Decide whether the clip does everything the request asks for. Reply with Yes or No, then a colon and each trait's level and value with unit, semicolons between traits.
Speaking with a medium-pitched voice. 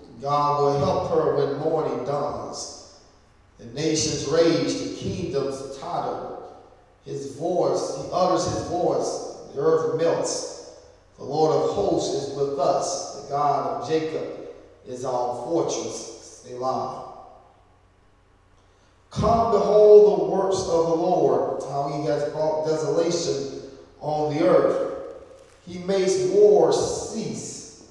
Yes: medium, 160 Hz